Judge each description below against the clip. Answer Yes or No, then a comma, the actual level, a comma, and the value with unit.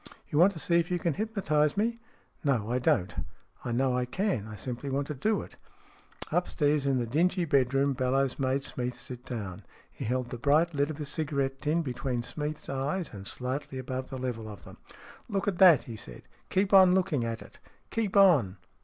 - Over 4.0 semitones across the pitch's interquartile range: Yes, average, 5.2 semitones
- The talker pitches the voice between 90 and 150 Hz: Yes, medium, 140 Hz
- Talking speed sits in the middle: No, fast, 215 wpm